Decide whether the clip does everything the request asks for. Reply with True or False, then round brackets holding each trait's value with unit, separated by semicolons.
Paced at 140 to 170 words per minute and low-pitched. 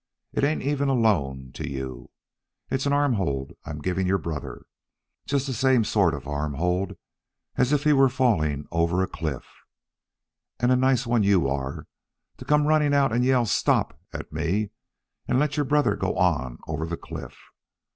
False (180 wpm; 105 Hz)